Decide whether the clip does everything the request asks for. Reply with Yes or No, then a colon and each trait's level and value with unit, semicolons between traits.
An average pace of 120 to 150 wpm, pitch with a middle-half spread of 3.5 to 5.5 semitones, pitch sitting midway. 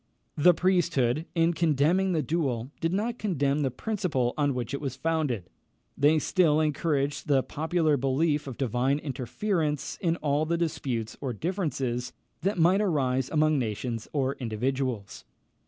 Yes: average, 145 wpm; average, 4.2 semitones; medium, 145 Hz